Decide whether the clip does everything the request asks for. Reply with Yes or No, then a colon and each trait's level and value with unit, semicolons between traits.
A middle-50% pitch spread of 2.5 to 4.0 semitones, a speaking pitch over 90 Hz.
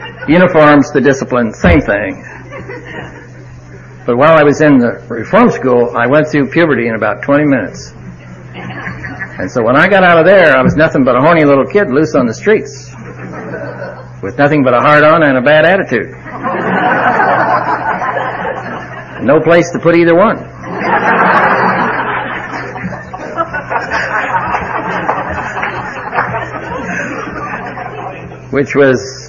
No: average, 4.7 semitones; low, 135 Hz